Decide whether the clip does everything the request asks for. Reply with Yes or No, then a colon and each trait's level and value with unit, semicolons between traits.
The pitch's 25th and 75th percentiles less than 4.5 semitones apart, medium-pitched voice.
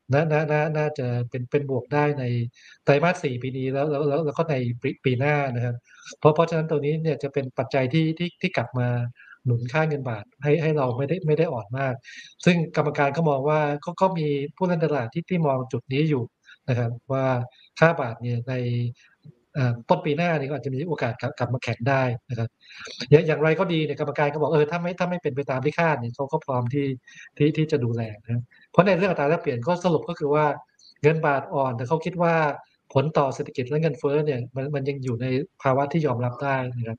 Yes: average, 3.2 semitones; medium, 145 Hz